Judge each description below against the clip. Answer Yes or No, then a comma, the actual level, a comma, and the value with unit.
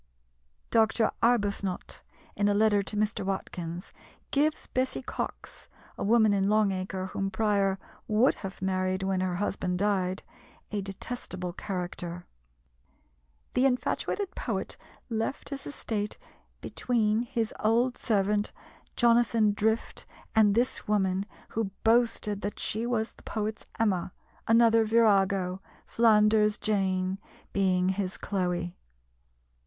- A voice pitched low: No, high, 205 Hz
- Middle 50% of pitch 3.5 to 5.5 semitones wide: No, average, 2.9 semitones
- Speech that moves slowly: Yes, slow, 115 wpm